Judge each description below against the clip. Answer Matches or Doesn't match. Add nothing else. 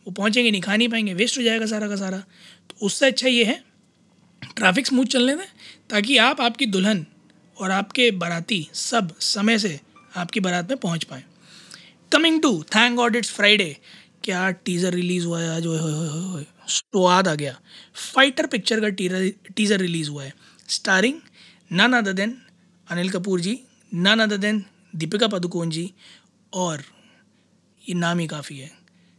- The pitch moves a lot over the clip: Doesn't match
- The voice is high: Matches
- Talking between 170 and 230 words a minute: Doesn't match